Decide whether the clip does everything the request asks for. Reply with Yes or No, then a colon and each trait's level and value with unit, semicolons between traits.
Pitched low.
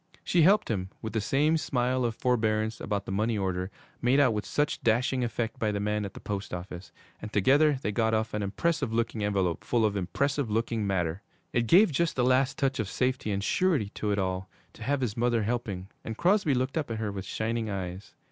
Yes: low, 110 Hz